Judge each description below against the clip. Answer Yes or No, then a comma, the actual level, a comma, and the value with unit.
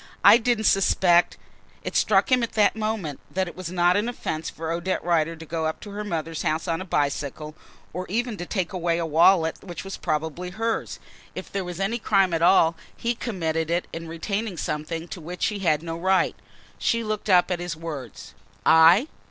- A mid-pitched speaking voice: Yes, medium, 175 Hz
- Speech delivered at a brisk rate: Yes, fast, 210 wpm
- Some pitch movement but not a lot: Yes, average, 3.4 semitones